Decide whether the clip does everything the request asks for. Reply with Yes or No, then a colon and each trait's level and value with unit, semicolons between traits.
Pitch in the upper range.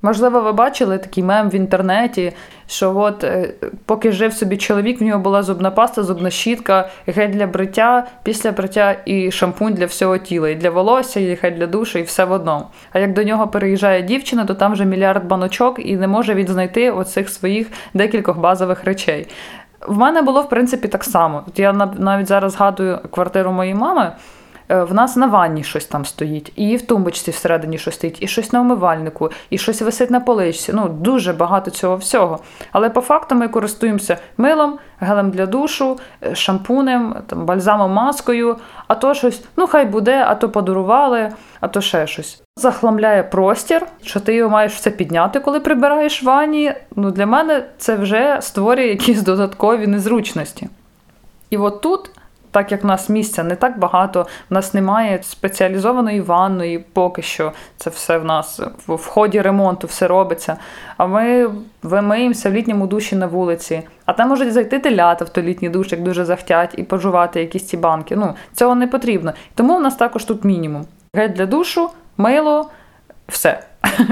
Yes: high, 205 Hz